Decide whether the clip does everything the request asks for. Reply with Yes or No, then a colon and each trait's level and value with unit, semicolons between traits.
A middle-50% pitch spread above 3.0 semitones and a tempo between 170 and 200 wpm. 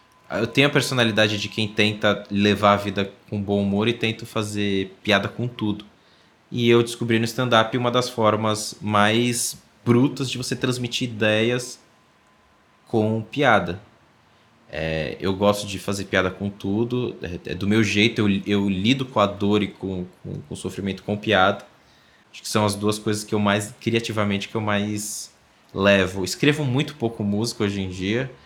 No: average, 2.7 semitones; average, 175 wpm